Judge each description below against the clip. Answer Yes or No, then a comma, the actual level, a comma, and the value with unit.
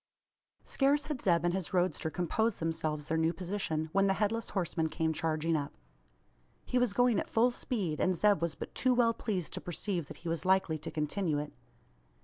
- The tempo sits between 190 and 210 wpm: Yes, average, 195 wpm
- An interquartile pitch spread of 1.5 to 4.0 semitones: No, average, 4.6 semitones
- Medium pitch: Yes, medium, 180 Hz